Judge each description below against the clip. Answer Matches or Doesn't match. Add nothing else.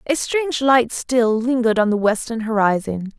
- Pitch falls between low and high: Doesn't match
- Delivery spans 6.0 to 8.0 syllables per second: Doesn't match